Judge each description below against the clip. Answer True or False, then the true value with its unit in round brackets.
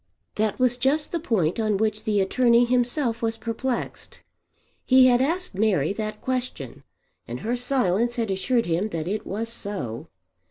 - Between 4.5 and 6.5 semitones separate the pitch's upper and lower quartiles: False (3.7 semitones)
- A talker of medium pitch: False (225 Hz)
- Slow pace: False (160 wpm)